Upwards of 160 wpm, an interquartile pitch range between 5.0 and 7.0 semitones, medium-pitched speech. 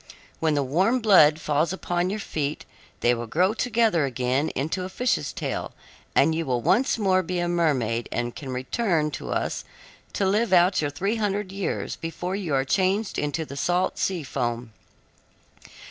Yes: average, 175 wpm; wide, 5.5 semitones; medium, 170 Hz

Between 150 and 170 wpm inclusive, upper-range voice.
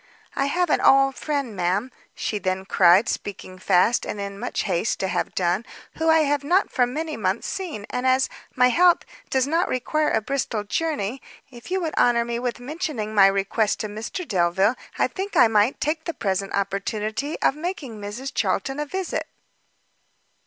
No: average, 180 wpm; high, 240 Hz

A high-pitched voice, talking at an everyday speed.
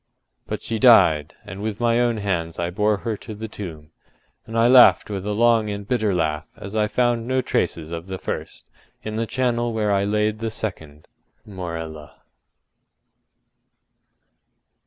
No: low, 105 Hz; average, 160 wpm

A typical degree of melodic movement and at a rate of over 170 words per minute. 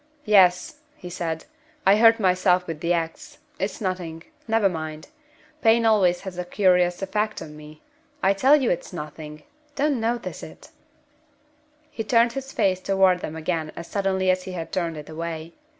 No: average, 4.1 semitones; average, 165 wpm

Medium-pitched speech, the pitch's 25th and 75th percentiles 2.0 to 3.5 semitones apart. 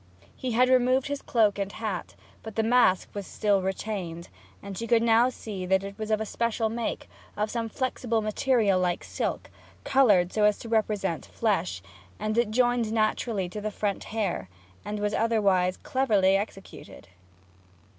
No: high, 215 Hz; average, 2.9 semitones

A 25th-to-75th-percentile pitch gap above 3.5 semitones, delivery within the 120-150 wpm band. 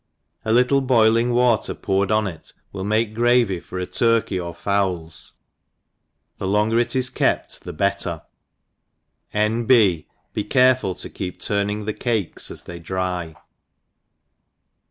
Yes: average, 4.1 semitones; average, 145 wpm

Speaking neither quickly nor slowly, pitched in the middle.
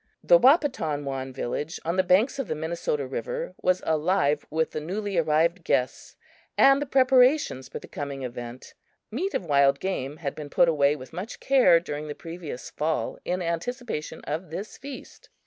Yes: average, 170 wpm; medium, 165 Hz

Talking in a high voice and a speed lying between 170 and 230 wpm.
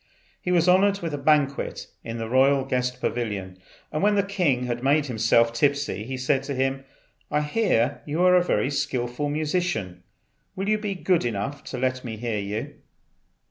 No: low, 135 Hz; average, 180 wpm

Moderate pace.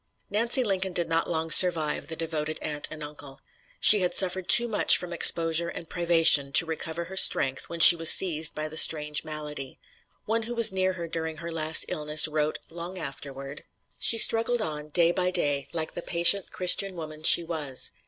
Yes: average, 190 wpm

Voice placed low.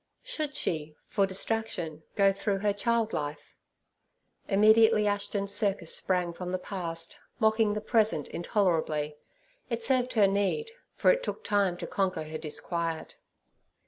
No: high, 200 Hz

